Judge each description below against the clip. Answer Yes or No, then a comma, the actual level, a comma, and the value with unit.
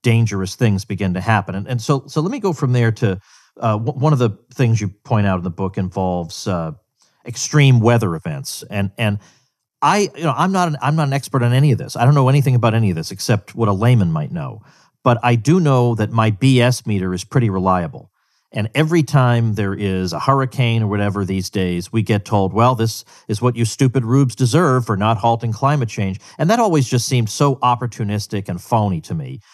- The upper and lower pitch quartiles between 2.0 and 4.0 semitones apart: No, average, 4.7 semitones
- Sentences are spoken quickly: Yes, fast, 225 wpm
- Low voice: Yes, low, 120 Hz